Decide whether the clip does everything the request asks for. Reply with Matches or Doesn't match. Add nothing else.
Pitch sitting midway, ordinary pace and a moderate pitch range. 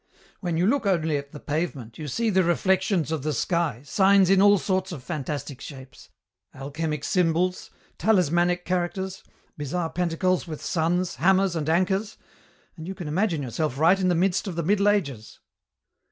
Matches